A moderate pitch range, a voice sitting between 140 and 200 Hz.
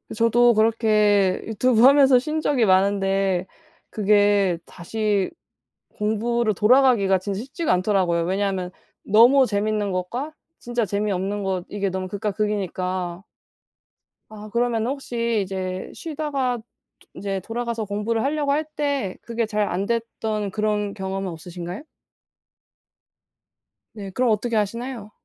No: average, 3.5 semitones; high, 210 Hz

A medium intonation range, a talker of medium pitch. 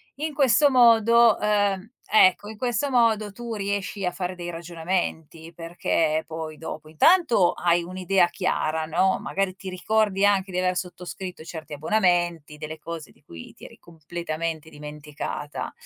Yes: average, 4.2 semitones; medium, 180 Hz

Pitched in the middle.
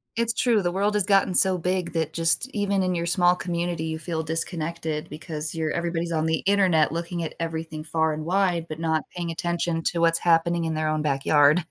Yes: medium, 165 Hz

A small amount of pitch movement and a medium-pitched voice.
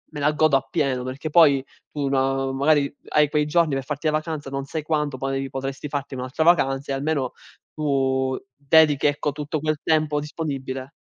Yes: narrow, 2.2 semitones; medium, 145 Hz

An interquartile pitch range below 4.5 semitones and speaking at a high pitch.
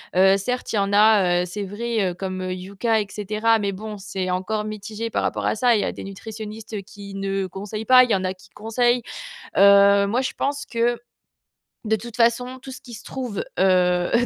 Yes: average, 3.0 semitones; high, 210 Hz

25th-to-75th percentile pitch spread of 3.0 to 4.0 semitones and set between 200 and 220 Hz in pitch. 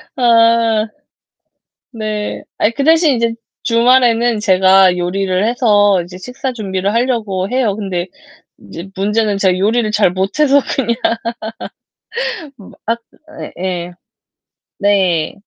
Yes: average, 3.7 semitones; high, 210 Hz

